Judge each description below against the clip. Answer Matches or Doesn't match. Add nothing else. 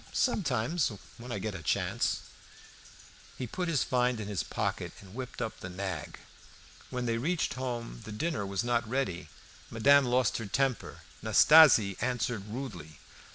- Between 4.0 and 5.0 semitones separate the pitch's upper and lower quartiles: Matches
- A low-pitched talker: Matches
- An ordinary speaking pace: Matches